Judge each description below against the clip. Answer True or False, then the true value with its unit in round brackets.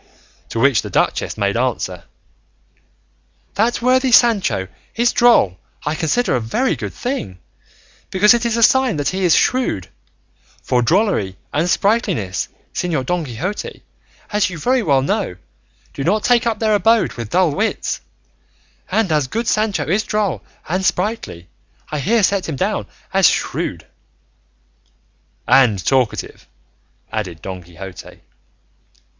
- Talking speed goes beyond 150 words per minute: False (140 wpm)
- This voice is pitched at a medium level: True (180 Hz)